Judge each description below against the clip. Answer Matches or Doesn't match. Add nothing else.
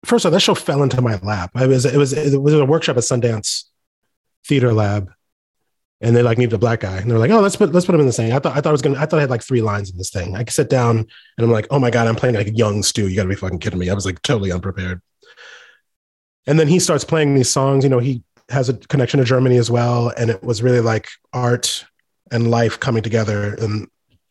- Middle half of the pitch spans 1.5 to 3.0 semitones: Doesn't match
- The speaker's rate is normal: Doesn't match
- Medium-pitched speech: Doesn't match